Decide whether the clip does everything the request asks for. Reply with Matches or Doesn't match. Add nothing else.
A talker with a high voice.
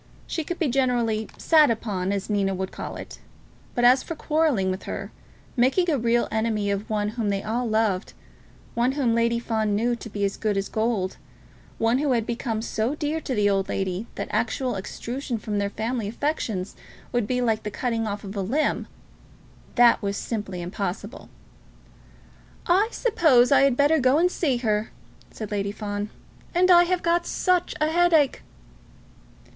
Matches